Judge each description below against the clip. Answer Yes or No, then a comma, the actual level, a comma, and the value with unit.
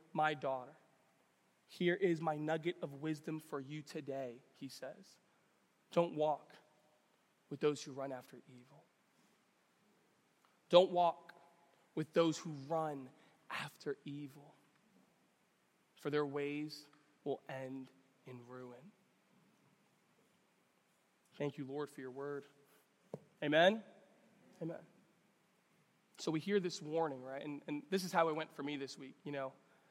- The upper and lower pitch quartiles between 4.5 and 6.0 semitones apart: No, average, 3.4 semitones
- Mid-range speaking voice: Yes, medium, 150 Hz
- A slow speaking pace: Yes, slow, 125 wpm